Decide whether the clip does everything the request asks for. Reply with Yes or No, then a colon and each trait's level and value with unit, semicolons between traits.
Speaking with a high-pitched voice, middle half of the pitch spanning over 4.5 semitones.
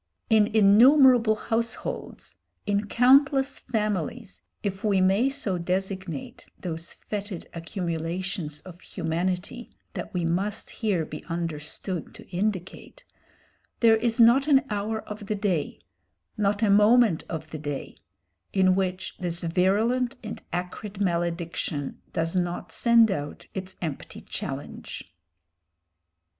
No: high, 195 Hz; average, 4.2 semitones